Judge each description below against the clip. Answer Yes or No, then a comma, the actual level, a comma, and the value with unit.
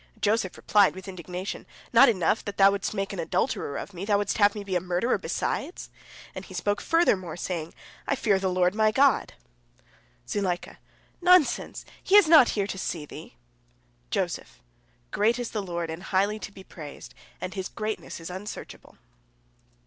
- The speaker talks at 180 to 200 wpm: No, average, 170 wpm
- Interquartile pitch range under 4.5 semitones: Yes, average, 3.1 semitones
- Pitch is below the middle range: No, high, 195 Hz